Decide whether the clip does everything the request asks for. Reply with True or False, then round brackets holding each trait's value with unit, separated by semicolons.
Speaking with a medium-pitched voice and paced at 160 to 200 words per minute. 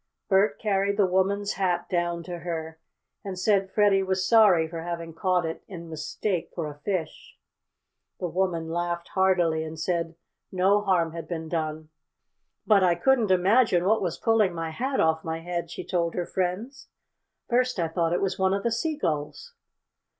True (180 Hz; 170 wpm)